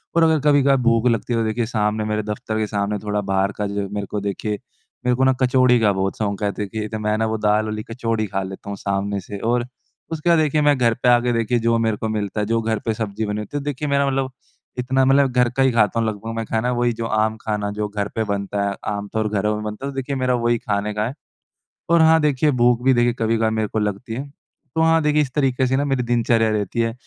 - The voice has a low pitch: Yes, low, 115 Hz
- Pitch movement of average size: Yes, average, 3.3 semitones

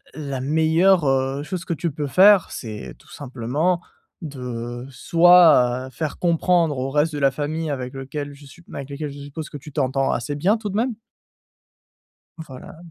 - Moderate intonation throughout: Yes, average, 3.7 semitones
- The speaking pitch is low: No, medium, 145 Hz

